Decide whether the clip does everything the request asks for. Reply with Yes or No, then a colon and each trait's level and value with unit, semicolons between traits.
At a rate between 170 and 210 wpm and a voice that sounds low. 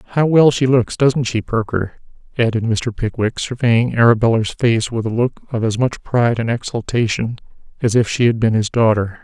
Yes: average, 190 wpm; low, 115 Hz